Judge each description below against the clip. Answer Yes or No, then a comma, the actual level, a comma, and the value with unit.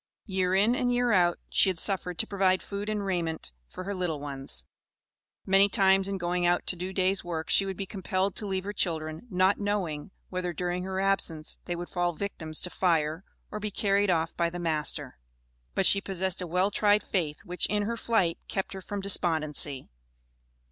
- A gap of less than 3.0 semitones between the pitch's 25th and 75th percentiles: Yes, narrow, 2.6 semitones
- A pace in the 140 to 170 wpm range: No, average, 195 wpm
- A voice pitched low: No, medium, 185 Hz